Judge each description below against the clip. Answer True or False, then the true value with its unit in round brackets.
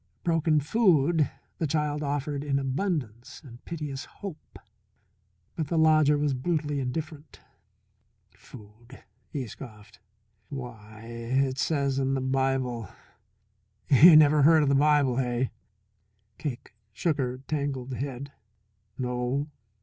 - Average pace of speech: False (115 wpm)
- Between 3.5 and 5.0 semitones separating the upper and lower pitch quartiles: False (3.1 semitones)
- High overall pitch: False (140 Hz)